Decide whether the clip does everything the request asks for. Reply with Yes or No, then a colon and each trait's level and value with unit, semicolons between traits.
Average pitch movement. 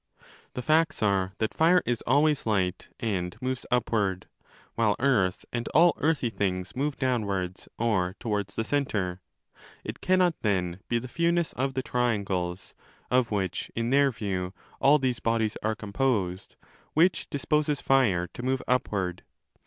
No: wide, 5.8 semitones